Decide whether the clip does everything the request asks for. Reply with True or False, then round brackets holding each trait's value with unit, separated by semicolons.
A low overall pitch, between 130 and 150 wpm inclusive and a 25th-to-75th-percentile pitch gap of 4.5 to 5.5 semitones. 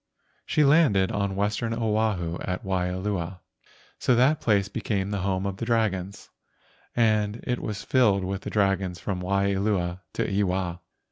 False (100 Hz; 145 wpm; 2.6 semitones)